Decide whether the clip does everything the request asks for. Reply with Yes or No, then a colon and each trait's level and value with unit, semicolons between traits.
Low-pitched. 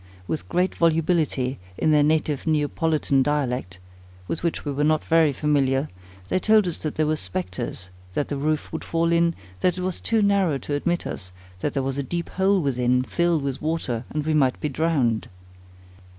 No: medium, 150 Hz